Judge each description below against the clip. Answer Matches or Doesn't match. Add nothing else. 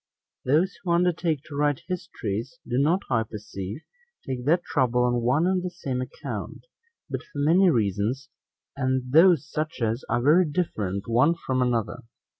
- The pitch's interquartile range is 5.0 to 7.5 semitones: Matches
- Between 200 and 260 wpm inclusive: Doesn't match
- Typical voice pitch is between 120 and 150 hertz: Matches